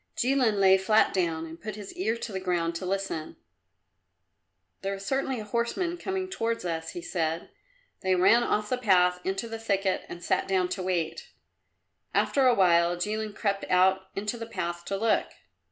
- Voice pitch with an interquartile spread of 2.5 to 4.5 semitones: Yes, average, 3.9 semitones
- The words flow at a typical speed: Yes, average, 180 wpm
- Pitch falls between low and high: No, high, 195 Hz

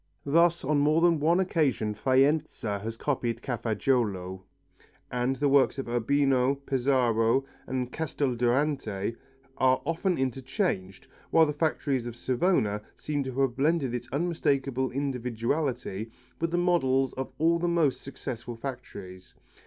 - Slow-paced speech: Yes, slow, 130 wpm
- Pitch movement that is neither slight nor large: Yes, average, 3.8 semitones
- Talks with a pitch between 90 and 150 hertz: Yes, low, 135 Hz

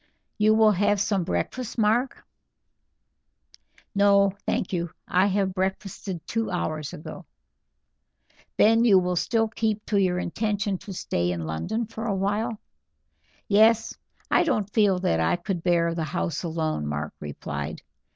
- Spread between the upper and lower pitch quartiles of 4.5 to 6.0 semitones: No, average, 3.9 semitones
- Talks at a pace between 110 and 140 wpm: Yes, slow, 135 wpm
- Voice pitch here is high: Yes, high, 195 Hz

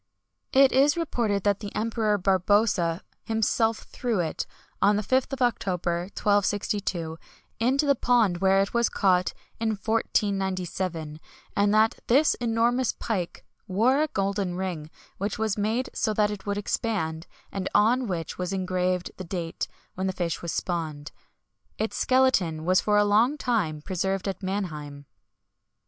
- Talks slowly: No, average, 150 wpm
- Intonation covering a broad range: No, average, 3.7 semitones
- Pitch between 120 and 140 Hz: No, high, 200 Hz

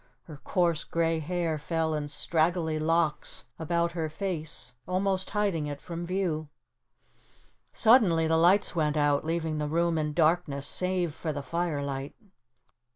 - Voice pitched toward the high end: No, medium, 165 Hz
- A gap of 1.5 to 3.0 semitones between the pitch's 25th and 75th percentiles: Yes, narrow, 2.4 semitones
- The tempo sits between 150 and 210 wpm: No, average, 140 wpm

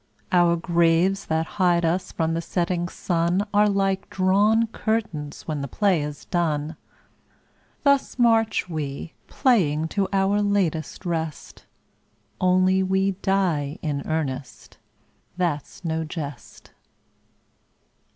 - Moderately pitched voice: Yes, medium, 175 Hz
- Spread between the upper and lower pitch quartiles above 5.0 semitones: No, average, 3.5 semitones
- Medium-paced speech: No, slow, 110 wpm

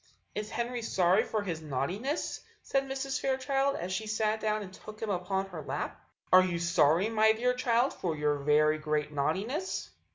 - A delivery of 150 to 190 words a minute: Yes, average, 175 wpm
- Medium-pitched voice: No, high, 205 Hz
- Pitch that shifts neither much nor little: No, wide, 6.7 semitones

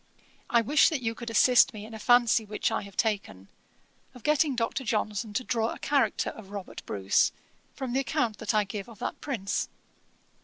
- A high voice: Yes, high, 225 Hz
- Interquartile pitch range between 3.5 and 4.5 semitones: No, average, 3.1 semitones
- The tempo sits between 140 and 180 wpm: No, average, 195 wpm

